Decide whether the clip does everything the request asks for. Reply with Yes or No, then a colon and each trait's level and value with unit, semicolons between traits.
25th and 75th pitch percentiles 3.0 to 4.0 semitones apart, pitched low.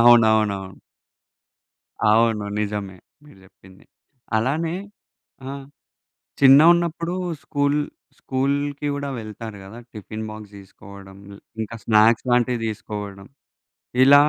No: average, 5.3 semitones; low, 110 Hz